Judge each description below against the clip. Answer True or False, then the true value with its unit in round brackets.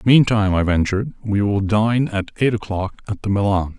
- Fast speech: False (190 wpm)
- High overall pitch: False (105 Hz)